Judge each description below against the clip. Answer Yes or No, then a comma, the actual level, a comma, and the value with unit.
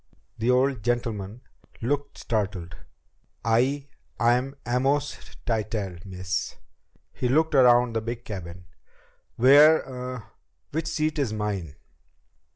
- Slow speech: Yes, slow, 105 wpm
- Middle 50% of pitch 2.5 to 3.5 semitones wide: No, average, 4.3 semitones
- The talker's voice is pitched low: Yes, low, 120 Hz